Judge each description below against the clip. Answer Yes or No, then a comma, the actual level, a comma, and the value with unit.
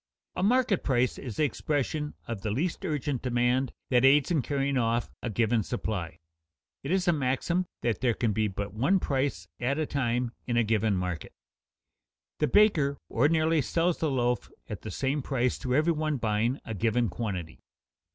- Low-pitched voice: Yes, low, 130 Hz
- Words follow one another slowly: No, average, 180 wpm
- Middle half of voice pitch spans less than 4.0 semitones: No, average, 4.7 semitones